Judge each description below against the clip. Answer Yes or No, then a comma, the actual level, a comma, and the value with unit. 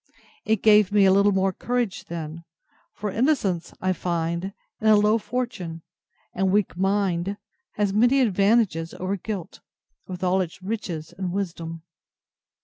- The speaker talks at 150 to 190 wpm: No, average, 140 wpm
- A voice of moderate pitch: No, high, 195 Hz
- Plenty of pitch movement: No, average, 3.2 semitones